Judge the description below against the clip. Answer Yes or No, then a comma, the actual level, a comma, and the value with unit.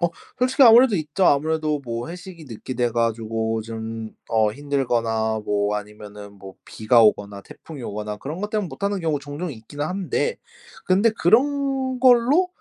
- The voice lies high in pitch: No, medium, 145 Hz